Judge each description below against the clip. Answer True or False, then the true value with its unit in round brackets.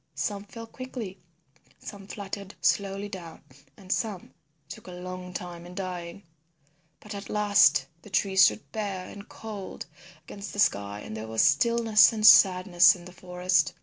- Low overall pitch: False (190 Hz)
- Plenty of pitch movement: False (2.5 semitones)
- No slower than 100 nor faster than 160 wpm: True (155 wpm)